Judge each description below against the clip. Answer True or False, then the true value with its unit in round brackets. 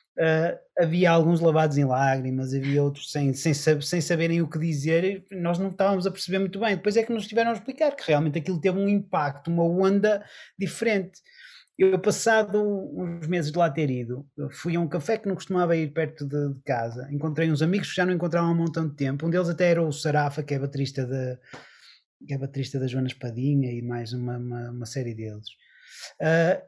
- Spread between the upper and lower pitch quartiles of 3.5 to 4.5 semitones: False (5.2 semitones)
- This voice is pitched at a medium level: True (165 Hz)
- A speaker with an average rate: False (205 wpm)